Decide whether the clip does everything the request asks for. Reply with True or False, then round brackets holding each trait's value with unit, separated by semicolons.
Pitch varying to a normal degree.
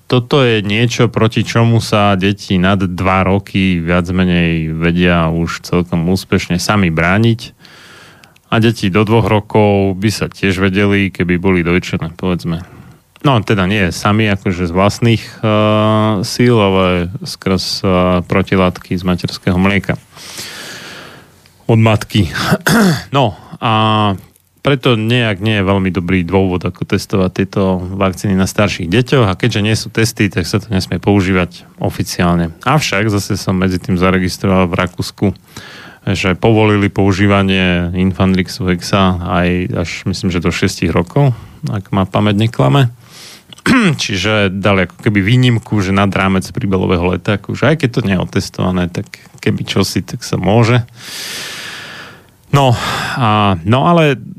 True (3.1 semitones)